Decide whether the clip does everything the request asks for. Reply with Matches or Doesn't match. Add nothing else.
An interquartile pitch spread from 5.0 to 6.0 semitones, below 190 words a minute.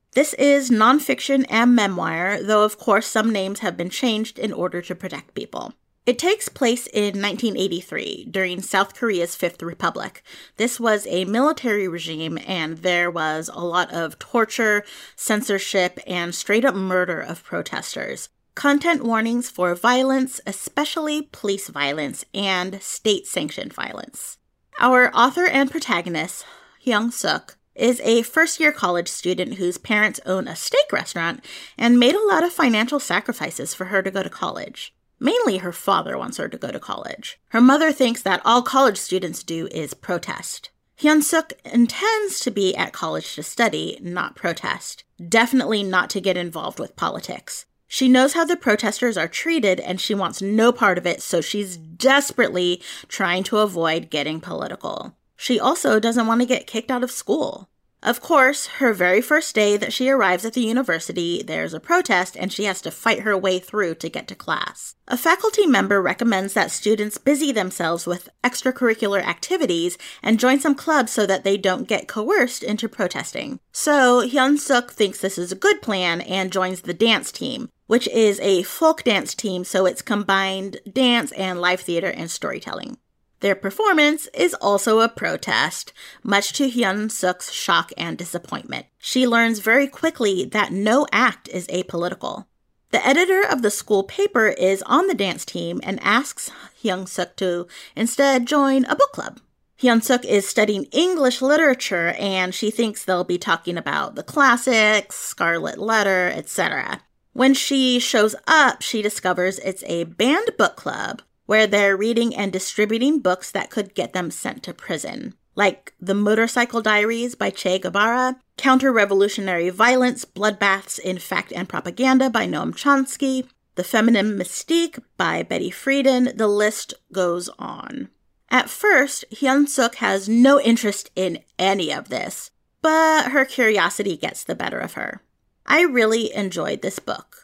Matches